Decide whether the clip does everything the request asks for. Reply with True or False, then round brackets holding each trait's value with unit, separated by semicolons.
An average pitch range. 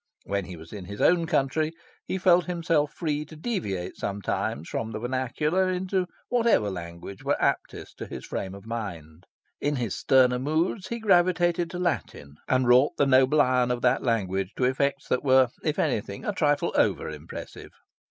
False (8.5 semitones)